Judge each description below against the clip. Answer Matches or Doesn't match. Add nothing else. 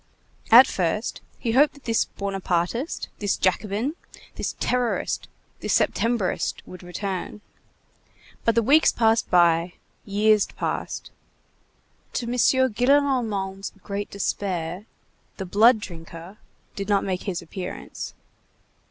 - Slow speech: Matches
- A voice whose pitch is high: Matches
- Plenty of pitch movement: Doesn't match